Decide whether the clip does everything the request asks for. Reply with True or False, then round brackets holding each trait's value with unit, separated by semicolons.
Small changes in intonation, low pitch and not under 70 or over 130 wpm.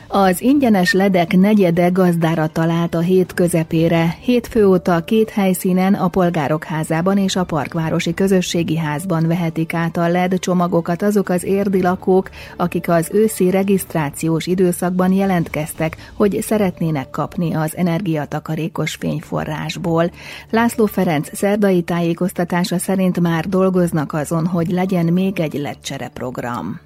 False (2.3 semitones; 180 Hz; 125 wpm)